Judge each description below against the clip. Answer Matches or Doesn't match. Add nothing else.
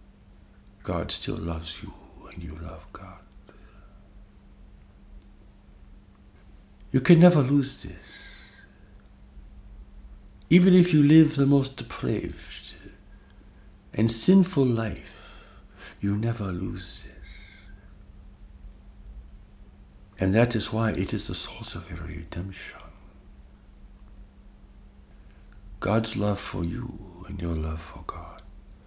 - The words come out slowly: Matches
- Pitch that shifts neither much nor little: Doesn't match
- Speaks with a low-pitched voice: Matches